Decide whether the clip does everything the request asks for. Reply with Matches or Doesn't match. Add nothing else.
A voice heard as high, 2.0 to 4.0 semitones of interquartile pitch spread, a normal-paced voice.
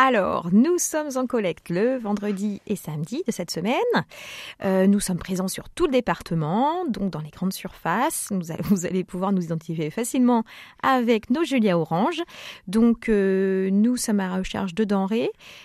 Doesn't match